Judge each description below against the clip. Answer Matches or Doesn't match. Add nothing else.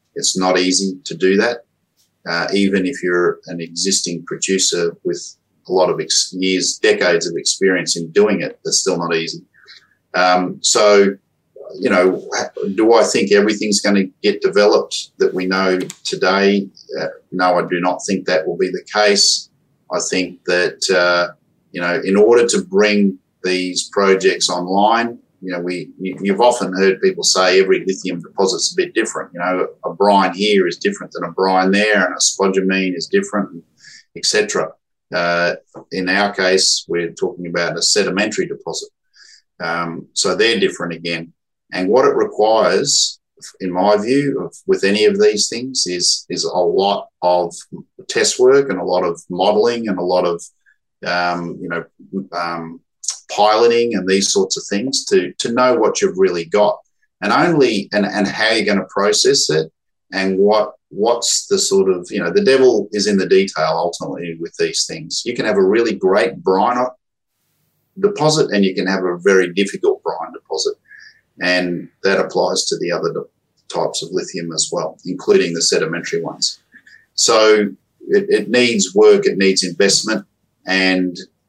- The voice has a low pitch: Matches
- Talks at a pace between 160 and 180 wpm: Matches